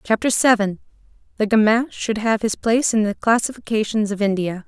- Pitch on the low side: No, high, 215 Hz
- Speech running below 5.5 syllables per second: No, 5.6 syllables/s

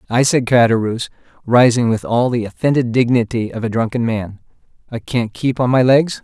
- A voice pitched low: Yes, low, 120 Hz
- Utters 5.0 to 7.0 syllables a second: Yes, 5.4 syllables/s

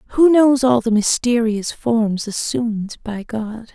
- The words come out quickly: No, average, 145 wpm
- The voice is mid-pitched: No, high, 230 Hz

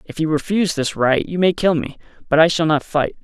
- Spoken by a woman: No, male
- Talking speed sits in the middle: No, fast, 260 wpm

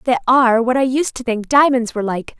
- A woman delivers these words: Yes, female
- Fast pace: Yes, fast, 250 wpm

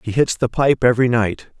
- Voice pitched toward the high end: No, low, 120 Hz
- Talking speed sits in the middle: No, fast, 225 wpm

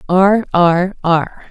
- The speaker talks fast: No, slow, 120 wpm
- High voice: No, medium, 180 Hz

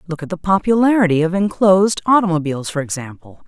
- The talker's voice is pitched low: No, medium, 180 Hz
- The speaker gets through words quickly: No, average, 155 wpm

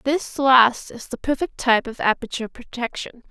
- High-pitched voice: Yes, very high, 250 Hz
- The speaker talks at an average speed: Yes, average, 165 wpm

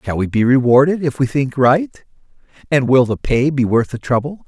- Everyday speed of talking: No, fast, 215 wpm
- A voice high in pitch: No, low, 135 Hz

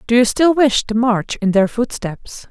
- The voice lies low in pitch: No, high, 230 Hz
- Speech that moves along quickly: Yes, fast, 215 wpm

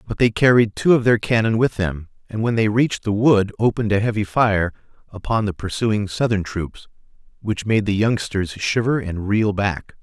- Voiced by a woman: No, male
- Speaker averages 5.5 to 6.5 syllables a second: No, 5.0 syllables/s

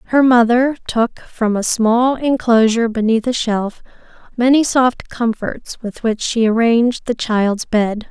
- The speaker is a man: No, female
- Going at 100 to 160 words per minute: Yes, average, 150 wpm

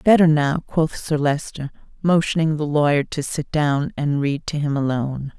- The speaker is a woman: Yes, female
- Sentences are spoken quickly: No, average, 180 wpm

